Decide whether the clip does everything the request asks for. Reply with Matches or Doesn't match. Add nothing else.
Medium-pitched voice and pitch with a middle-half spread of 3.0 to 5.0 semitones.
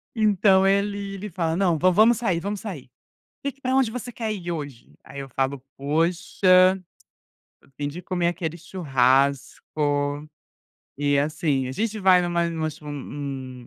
Doesn't match